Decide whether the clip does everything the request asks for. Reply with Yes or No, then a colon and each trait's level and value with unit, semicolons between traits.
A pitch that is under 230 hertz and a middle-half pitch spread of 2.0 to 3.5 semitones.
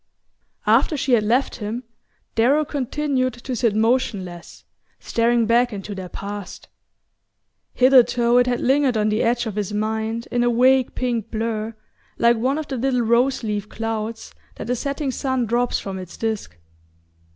No: high, 235 Hz; average, 2.8 semitones